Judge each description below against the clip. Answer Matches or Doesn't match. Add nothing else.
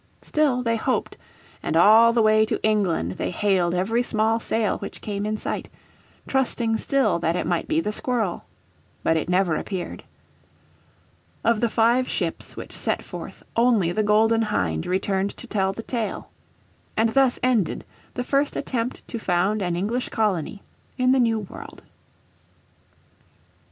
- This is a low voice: Doesn't match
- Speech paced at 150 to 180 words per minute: Matches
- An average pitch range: Matches